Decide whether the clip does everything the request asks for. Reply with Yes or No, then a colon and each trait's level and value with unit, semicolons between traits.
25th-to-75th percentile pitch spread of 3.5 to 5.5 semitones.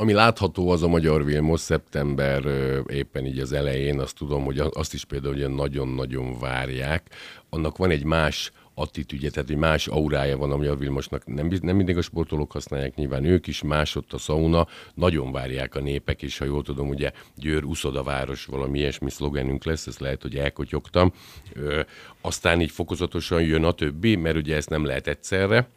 No: average, 3.0 semitones